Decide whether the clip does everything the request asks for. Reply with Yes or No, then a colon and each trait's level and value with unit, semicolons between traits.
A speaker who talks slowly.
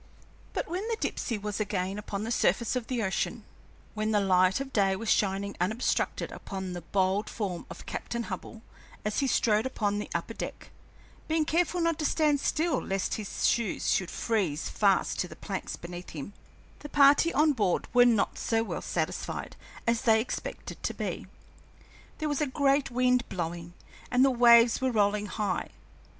No: average, 175 wpm